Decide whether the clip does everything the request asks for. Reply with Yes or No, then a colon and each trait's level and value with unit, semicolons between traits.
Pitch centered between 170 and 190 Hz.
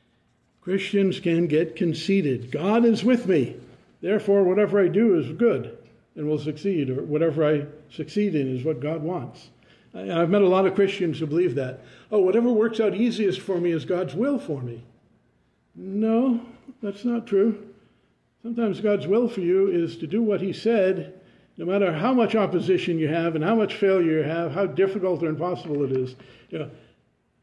Yes: medium, 185 Hz